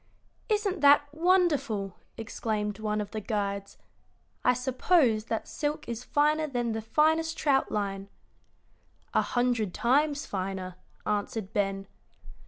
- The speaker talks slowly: Yes, slow, 120 wpm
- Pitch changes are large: Yes, wide, 6.2 semitones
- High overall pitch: Yes, high, 235 Hz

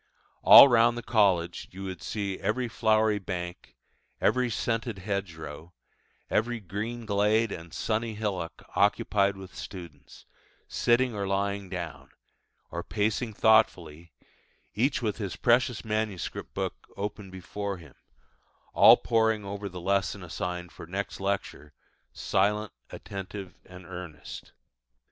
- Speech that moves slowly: Yes, slow, 120 wpm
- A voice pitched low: Yes, low, 100 Hz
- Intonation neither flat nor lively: Yes, average, 3.3 semitones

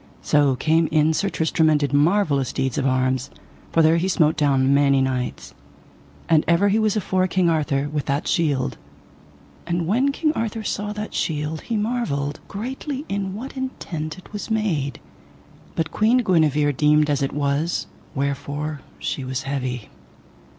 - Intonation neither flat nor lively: No, wide, 5.9 semitones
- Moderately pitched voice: Yes, medium, 155 Hz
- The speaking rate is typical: Yes, average, 160 wpm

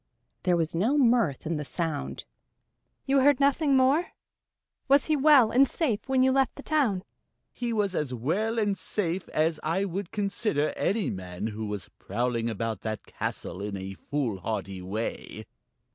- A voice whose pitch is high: No, medium, 180 Hz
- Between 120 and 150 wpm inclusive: No, average, 160 wpm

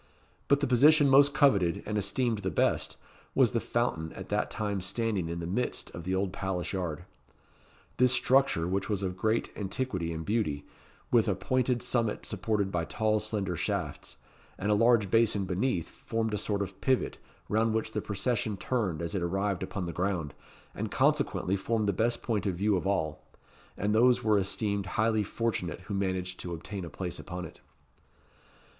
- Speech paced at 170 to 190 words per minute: Yes, average, 180 wpm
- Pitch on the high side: No, low, 100 Hz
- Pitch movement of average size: Yes, average, 3.7 semitones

